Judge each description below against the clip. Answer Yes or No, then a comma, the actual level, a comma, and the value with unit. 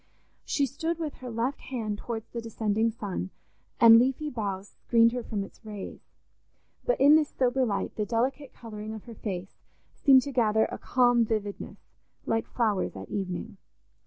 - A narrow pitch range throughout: No, average, 3.3 semitones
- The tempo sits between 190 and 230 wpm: No, average, 165 wpm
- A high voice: Yes, high, 230 Hz